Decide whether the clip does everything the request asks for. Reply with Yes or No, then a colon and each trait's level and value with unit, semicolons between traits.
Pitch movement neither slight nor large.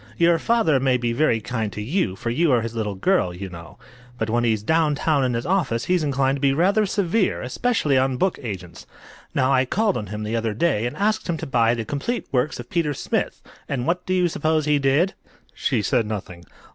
No: wide, 6.8 semitones